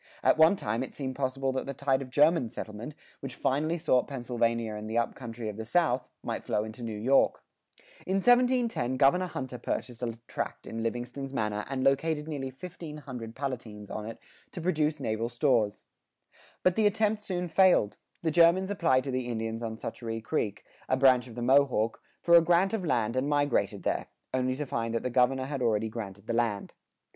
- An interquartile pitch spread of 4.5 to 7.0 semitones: Yes, average, 4.8 semitones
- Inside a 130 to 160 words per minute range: No, average, 195 wpm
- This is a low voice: Yes, low, 130 Hz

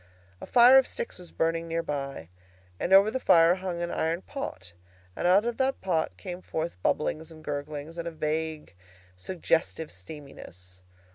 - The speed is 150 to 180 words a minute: Yes, average, 165 wpm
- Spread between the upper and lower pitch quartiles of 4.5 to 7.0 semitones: No, average, 3.5 semitones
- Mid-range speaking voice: Yes, medium, 165 Hz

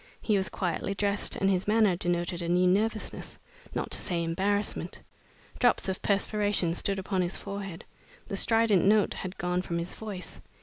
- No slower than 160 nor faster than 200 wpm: Yes, average, 170 wpm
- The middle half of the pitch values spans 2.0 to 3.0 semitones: Yes, narrow, 2.4 semitones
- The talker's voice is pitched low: No, high, 195 Hz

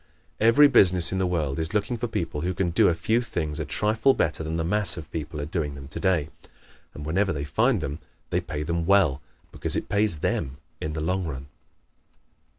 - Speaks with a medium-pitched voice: No, very low, 85 Hz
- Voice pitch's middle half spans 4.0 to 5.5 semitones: Yes, average, 4.9 semitones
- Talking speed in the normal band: No, fast, 210 wpm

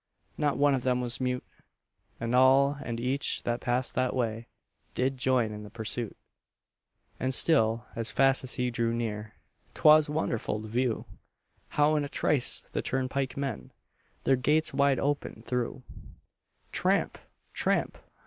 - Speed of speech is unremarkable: Yes, average, 150 wpm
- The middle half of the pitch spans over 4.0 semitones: No, average, 2.9 semitones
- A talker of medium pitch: No, low, 125 Hz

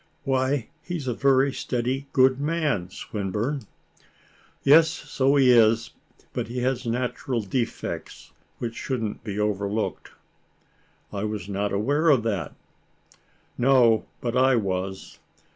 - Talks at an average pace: No, slow, 125 wpm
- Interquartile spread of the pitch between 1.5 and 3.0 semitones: No, average, 4.2 semitones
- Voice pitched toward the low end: Yes, low, 120 Hz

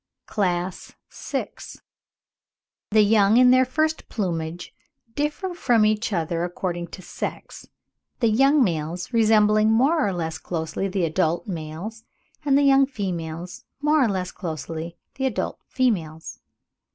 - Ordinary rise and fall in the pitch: No, wide, 6.6 semitones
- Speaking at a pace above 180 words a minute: No, slow, 135 wpm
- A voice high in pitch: Yes, high, 200 Hz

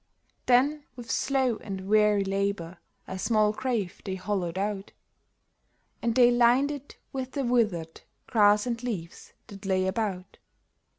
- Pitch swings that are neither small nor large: Yes, average, 4.1 semitones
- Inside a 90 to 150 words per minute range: Yes, slow, 135 wpm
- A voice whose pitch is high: Yes, high, 210 Hz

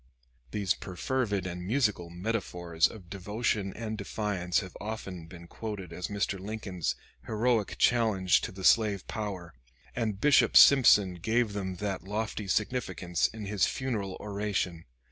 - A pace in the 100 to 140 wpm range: Yes, slow, 135 wpm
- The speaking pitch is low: Yes, low, 100 Hz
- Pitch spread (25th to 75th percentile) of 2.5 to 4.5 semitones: Yes, average, 3.2 semitones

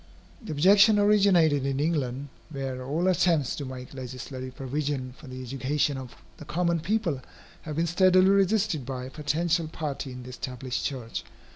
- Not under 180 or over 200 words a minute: No, average, 160 wpm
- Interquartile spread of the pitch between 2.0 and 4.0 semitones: No, average, 4.7 semitones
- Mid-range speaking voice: Yes, medium, 145 Hz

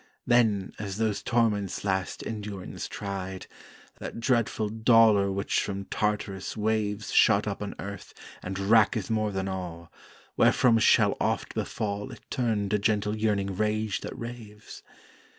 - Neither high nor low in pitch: No, low, 105 Hz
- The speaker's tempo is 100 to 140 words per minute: Yes, slow, 135 wpm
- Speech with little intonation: Yes, narrow, 1.9 semitones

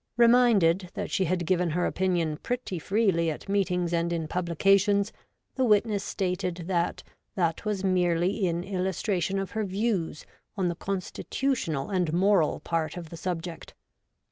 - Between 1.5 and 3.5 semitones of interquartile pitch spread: Yes, average, 2.8 semitones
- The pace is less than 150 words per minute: No, average, 155 wpm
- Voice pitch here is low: No, medium, 185 Hz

